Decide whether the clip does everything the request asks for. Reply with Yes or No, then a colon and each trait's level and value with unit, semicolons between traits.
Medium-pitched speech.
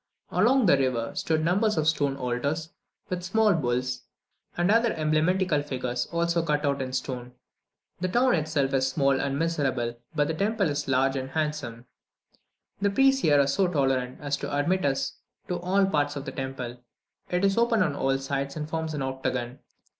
Yes: medium, 145 Hz